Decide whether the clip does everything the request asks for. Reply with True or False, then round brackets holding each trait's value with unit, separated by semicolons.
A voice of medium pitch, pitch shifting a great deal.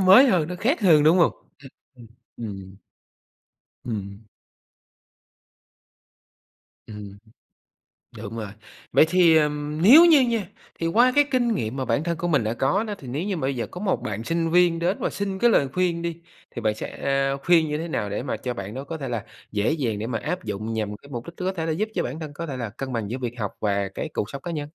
True (150 Hz; 7.5 semitones)